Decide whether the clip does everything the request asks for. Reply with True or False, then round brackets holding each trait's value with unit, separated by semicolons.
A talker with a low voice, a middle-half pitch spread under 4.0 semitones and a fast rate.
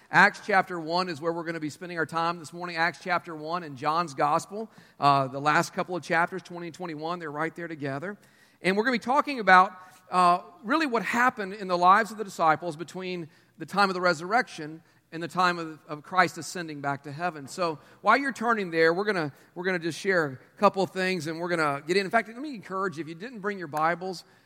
False (175 Hz; 2.8 semitones; 250 wpm)